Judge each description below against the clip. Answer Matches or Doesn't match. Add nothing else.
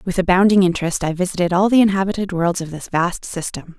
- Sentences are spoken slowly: Doesn't match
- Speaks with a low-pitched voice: Doesn't match